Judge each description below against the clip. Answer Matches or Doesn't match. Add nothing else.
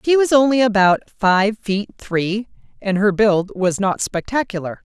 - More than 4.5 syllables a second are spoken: Doesn't match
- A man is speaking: Doesn't match